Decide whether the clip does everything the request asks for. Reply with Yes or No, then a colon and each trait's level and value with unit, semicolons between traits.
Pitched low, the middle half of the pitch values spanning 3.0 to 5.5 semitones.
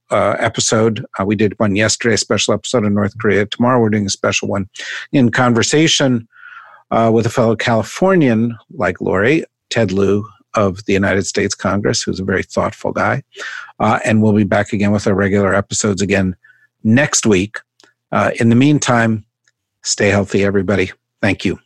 No: low, 110 Hz; narrow, 2.6 semitones